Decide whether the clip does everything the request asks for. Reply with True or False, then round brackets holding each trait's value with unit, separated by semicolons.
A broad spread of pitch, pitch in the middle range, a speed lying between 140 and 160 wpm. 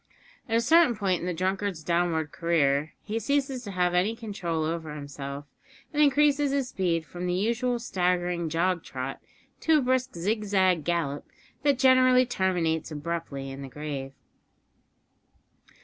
True (6.7 semitones; 180 Hz; 150 wpm)